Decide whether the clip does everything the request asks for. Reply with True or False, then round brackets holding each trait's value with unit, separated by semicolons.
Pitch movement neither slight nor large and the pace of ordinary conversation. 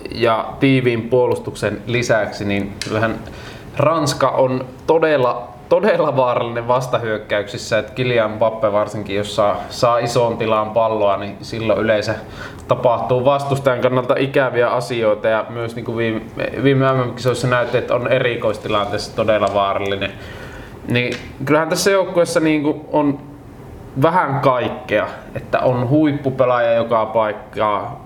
True (3.5 semitones; 115 wpm)